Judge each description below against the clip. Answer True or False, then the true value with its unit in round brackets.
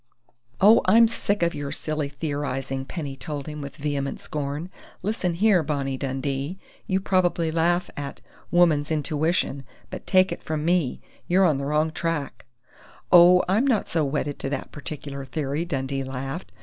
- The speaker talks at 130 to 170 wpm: True (160 wpm)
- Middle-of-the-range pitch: True (150 Hz)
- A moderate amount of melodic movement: True (4.0 semitones)